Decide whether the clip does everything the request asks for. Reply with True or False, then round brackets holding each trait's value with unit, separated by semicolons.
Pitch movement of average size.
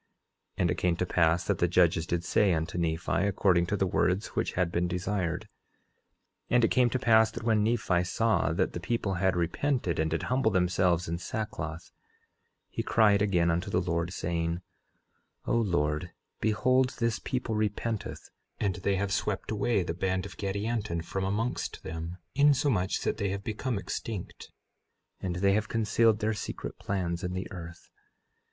True (3.9 semitones)